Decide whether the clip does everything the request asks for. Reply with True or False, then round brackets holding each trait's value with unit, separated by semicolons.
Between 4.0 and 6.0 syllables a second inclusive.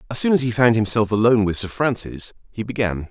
False (6.2 syllables/s)